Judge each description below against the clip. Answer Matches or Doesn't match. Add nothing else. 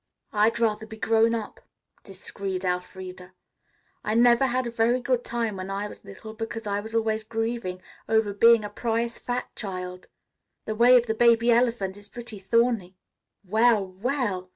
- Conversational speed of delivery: Matches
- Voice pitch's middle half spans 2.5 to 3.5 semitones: Matches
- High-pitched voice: Matches